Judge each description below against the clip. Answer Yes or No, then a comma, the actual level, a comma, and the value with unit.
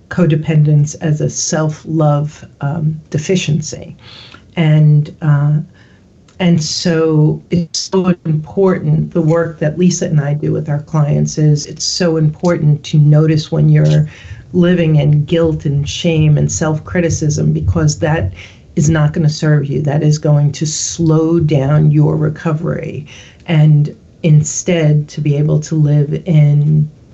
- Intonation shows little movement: Yes, narrow, 1.8 semitones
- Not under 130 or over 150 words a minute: Yes, slow, 135 wpm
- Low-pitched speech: No, medium, 155 Hz